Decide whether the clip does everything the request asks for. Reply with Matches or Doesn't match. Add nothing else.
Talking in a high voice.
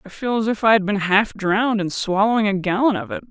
Matches